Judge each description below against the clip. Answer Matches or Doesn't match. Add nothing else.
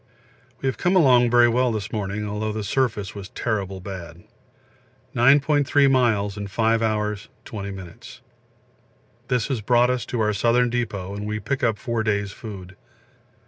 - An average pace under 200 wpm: Matches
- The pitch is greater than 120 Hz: Doesn't match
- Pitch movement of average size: Matches